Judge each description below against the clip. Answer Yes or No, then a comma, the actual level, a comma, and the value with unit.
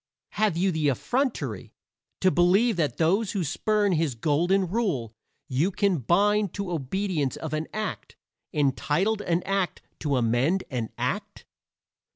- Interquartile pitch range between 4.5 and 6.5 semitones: Yes, wide, 5.4 semitones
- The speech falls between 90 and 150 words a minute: Yes, average, 140 wpm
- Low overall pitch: No, medium, 175 Hz